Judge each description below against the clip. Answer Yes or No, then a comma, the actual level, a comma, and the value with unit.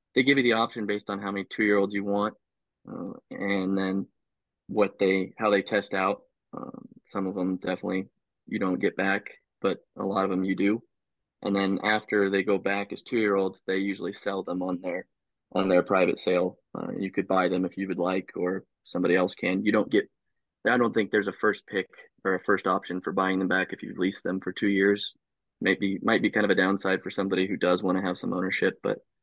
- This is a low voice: Yes, very low, 95 Hz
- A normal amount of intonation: No, narrow, 1.2 semitones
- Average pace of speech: No, fast, 225 wpm